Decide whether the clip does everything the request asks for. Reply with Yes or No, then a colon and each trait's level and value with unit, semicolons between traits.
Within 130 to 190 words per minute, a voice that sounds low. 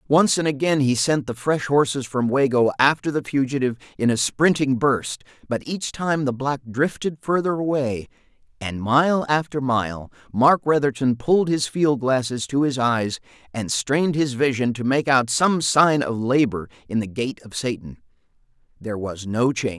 Yes: average, 175 wpm; low, 130 Hz